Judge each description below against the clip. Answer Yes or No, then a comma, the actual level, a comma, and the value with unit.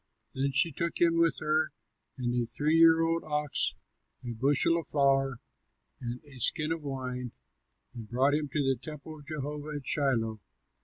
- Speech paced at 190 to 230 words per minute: No, average, 170 wpm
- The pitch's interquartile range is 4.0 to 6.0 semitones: No, average, 3.2 semitones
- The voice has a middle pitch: Yes, medium, 145 Hz